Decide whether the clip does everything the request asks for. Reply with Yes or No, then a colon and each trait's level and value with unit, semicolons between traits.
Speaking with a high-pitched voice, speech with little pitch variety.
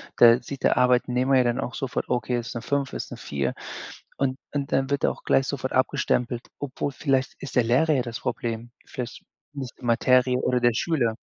No: low, 125 Hz; narrow, 2.0 semitones